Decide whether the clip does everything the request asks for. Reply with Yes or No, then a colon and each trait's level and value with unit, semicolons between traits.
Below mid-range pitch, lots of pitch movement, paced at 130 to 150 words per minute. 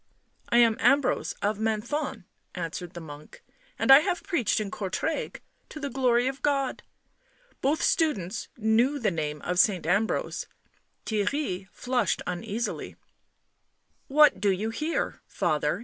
No: high, 225 Hz; wide, 6.4 semitones; average, 145 wpm